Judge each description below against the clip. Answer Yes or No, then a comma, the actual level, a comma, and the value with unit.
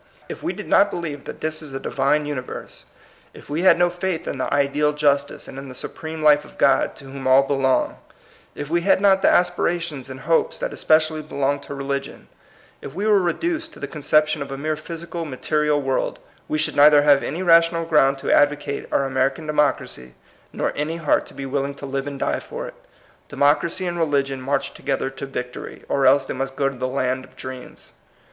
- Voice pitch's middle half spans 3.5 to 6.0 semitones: No, average, 3.0 semitones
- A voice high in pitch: No, medium, 145 Hz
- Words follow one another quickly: Yes, fast, 215 wpm